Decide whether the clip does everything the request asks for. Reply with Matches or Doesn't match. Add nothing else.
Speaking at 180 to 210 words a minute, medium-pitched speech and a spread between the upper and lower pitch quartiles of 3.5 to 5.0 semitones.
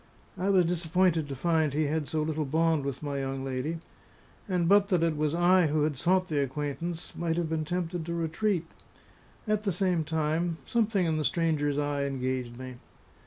Doesn't match